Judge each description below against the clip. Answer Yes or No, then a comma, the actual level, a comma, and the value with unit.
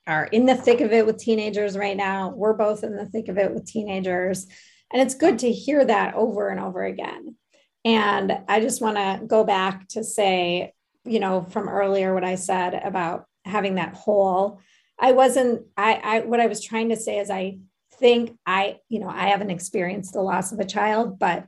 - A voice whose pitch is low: No, high, 210 Hz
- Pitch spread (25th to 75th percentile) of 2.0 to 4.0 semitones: Yes, average, 2.8 semitones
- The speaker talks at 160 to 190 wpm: No, fast, 205 wpm